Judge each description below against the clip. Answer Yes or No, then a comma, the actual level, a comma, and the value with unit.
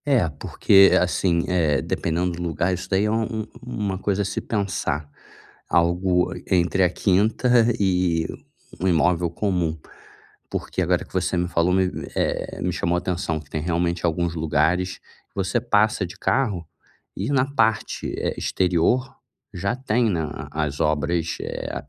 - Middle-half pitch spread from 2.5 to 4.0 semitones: Yes, average, 3.0 semitones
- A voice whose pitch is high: No, very low, 90 Hz